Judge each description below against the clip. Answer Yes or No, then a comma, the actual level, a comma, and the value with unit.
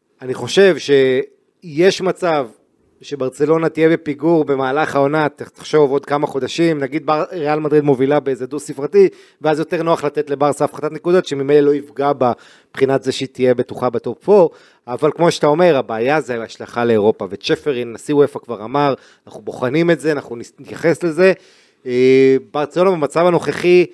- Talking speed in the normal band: No, fast, 155 wpm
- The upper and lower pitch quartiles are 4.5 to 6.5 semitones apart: No, average, 3.4 semitones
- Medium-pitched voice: Yes, medium, 145 Hz